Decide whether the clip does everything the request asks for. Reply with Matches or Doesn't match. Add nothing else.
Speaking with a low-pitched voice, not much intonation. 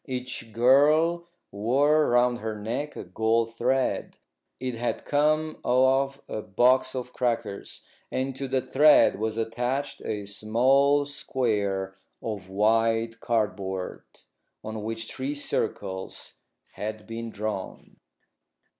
Doesn't match